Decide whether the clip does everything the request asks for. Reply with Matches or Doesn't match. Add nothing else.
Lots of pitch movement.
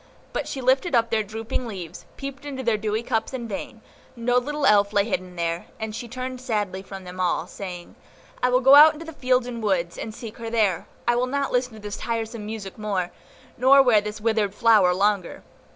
Doesn't match